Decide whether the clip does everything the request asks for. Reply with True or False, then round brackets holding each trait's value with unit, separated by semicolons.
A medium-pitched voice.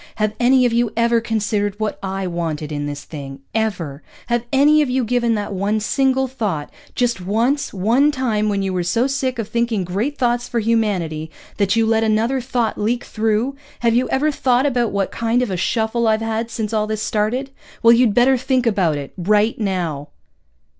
False (225 Hz)